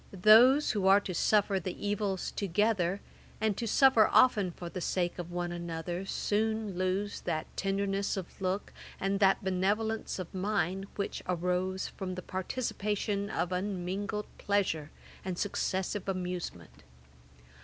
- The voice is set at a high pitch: Yes, high, 195 Hz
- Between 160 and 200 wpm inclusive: No, slow, 135 wpm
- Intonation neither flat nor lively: No, narrow, 2.2 semitones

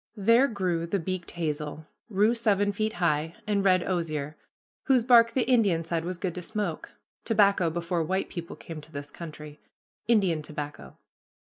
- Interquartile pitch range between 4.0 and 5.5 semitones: Yes, average, 4.4 semitones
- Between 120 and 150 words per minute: No, average, 160 wpm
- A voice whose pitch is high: No, medium, 180 Hz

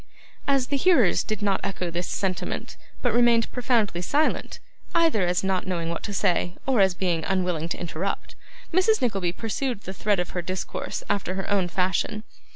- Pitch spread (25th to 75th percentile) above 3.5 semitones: Yes, average, 4.8 semitones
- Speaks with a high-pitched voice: Yes, high, 195 Hz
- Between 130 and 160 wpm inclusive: No, average, 175 wpm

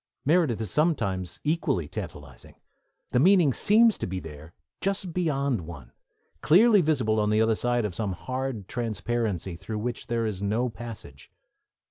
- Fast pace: No, average, 150 wpm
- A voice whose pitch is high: No, low, 115 Hz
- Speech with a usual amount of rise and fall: No, wide, 7.7 semitones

